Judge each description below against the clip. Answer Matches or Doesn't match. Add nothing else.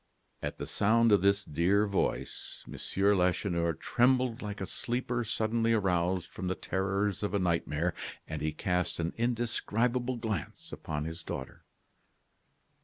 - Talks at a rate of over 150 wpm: Doesn't match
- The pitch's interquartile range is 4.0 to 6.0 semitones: Matches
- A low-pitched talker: Matches